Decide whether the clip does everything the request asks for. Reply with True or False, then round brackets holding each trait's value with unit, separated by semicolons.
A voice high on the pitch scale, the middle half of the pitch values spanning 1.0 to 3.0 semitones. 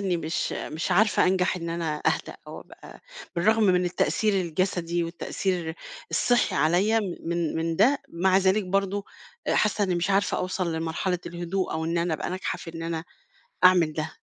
False (180 Hz; 2.5 semitones)